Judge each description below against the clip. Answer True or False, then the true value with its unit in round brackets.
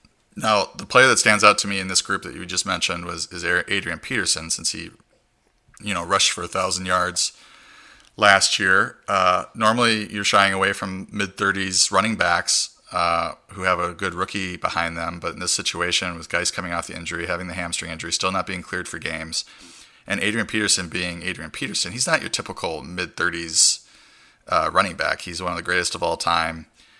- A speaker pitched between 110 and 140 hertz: False (95 Hz)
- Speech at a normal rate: True (195 wpm)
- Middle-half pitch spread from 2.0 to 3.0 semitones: True (2.7 semitones)